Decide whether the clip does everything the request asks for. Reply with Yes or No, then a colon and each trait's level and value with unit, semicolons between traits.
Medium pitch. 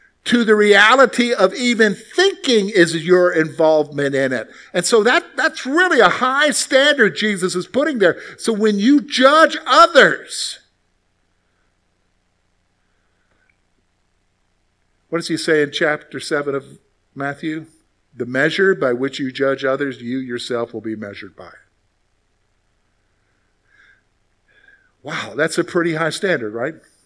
Yes: medium, 150 Hz